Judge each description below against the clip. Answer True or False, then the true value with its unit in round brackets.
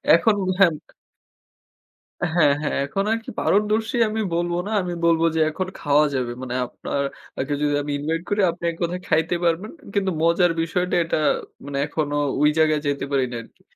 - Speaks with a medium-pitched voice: True (165 Hz)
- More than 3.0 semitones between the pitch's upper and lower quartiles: True (3.6 semitones)